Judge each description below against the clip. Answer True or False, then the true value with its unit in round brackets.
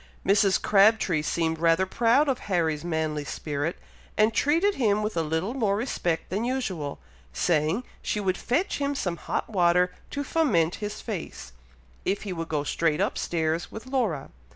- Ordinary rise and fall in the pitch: False (5.7 semitones)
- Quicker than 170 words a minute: False (165 wpm)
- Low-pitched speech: False (185 Hz)